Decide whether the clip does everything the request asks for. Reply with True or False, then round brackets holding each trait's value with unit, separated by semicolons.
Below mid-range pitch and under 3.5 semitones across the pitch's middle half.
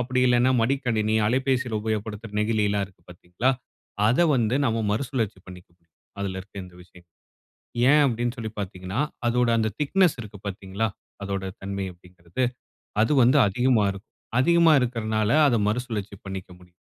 False (110 Hz; 4.2 semitones)